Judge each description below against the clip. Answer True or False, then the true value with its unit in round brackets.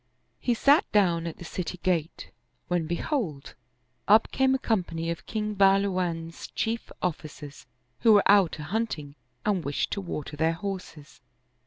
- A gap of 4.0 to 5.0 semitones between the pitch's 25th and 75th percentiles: True (4.3 semitones)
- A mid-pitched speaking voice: True (180 Hz)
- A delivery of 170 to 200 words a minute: False (155 wpm)